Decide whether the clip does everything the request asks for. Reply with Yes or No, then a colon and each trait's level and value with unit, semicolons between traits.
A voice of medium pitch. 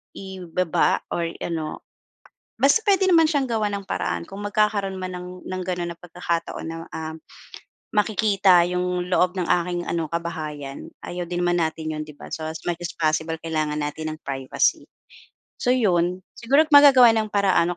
Yes: medium, 180 Hz